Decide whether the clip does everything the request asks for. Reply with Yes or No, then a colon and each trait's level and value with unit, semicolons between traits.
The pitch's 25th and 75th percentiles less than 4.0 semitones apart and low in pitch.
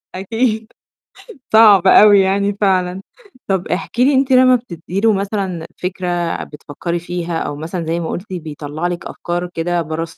No: average, 3.2 semitones; medium, 185 Hz